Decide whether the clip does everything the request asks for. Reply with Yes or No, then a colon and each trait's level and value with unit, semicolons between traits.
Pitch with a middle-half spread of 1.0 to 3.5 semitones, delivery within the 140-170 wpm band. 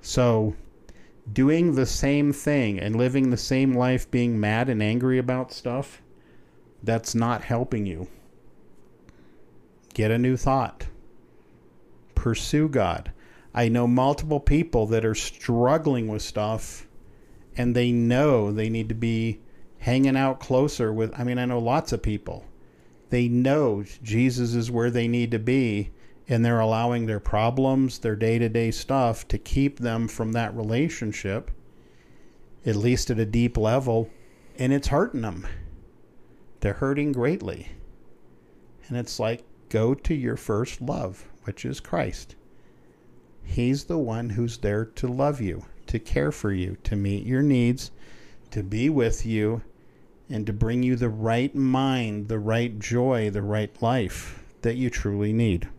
Yes: average, 3.1 semitones; average, 150 wpm